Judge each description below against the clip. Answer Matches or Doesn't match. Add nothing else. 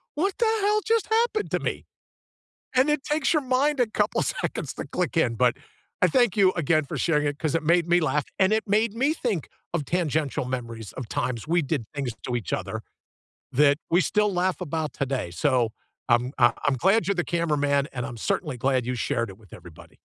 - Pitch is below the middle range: Doesn't match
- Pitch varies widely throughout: Matches